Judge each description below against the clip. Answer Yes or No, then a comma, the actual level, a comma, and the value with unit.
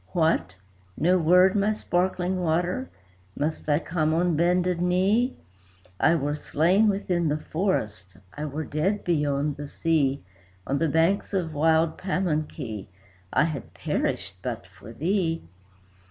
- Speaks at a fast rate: No, slow, 135 wpm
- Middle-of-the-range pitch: Yes, medium, 165 Hz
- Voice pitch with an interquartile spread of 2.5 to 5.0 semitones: Yes, average, 3.7 semitones